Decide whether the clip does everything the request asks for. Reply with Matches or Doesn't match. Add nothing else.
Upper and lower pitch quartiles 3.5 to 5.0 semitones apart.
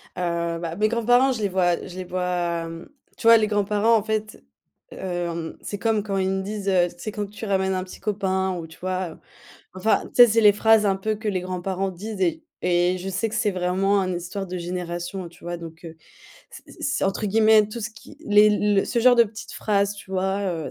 Doesn't match